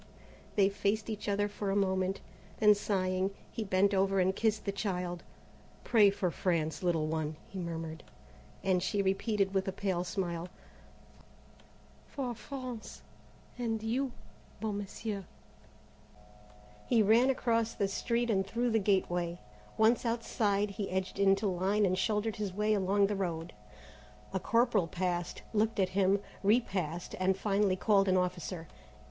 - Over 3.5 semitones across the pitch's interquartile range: No, narrow, 2.6 semitones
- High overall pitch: Yes, high, 195 Hz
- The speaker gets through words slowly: No, average, 145 wpm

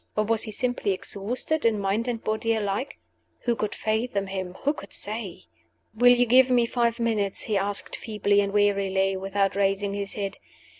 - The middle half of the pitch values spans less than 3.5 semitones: Yes, average, 2.8 semitones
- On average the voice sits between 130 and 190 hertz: No, high, 210 Hz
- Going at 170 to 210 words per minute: Yes, average, 180 wpm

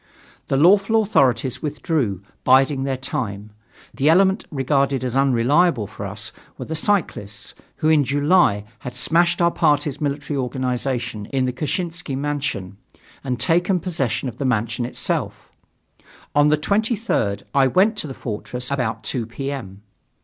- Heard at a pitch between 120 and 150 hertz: Yes, low, 135 Hz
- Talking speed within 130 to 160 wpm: Yes, average, 145 wpm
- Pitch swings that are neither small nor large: Yes, average, 4.5 semitones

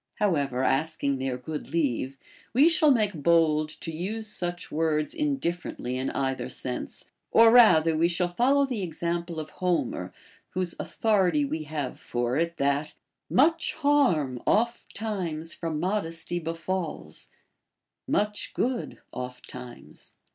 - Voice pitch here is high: No, medium, 165 Hz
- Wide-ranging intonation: Yes, wide, 5.8 semitones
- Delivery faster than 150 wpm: No, slow, 135 wpm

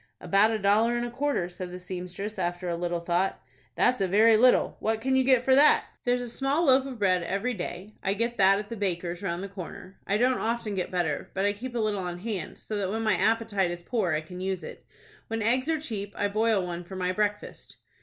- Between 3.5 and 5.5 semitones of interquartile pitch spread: Yes, average, 4.2 semitones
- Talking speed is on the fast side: Yes, fast, 245 wpm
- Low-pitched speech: No, high, 205 Hz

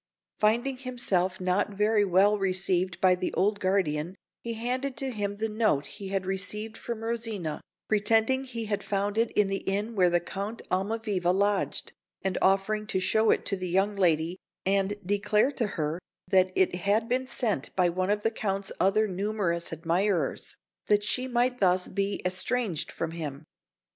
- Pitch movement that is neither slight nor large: Yes, average, 3.0 semitones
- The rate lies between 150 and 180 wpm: Yes, average, 170 wpm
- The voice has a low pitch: No, high, 200 Hz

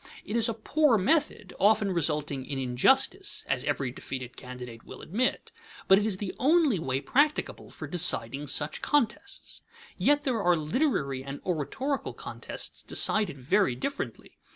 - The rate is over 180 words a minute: No, average, 150 wpm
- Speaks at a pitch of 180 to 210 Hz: Yes, high, 190 Hz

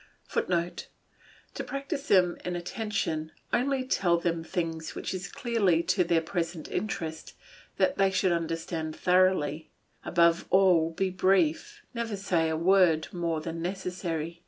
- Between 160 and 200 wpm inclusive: No, average, 140 wpm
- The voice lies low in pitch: No, medium, 175 Hz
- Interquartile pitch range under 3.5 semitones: Yes, average, 2.7 semitones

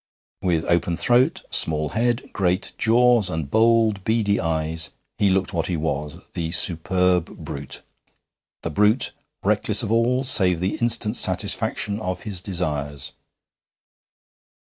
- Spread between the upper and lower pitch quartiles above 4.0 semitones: Yes, wide, 5.5 semitones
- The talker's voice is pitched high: No, very low, 95 Hz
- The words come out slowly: Yes, slow, 125 wpm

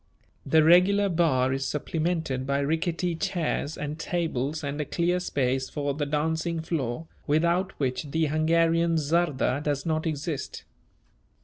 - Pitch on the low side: No, medium, 155 Hz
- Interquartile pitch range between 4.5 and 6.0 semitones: No, average, 2.9 semitones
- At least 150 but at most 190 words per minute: No, slow, 135 wpm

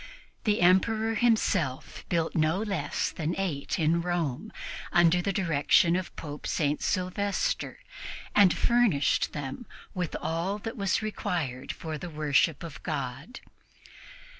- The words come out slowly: Yes, slow, 125 wpm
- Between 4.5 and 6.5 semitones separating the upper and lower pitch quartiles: Yes, average, 4.8 semitones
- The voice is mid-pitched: Yes, medium, 175 Hz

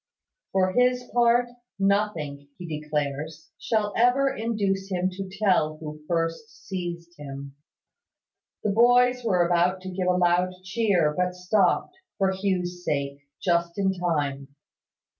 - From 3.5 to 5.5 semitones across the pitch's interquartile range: Yes, average, 3.9 semitones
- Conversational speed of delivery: No, slow, 130 wpm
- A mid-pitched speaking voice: Yes, medium, 180 Hz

